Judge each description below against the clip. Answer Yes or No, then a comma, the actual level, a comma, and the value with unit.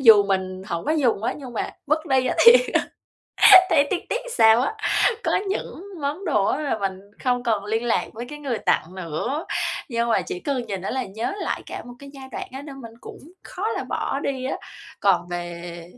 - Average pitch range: No, wide, 6.1 semitones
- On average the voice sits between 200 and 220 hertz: No, high, 245 Hz